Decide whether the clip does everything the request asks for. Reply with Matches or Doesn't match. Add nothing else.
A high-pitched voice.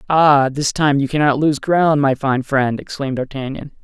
Doesn't match